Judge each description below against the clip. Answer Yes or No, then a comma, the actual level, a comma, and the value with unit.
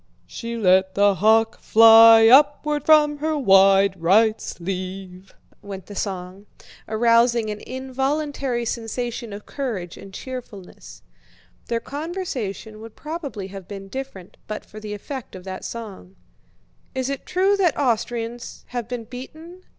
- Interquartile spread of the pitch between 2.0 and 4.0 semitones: No, average, 5.1 semitones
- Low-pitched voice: No, high, 225 Hz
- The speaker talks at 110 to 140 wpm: Yes, slow, 135 wpm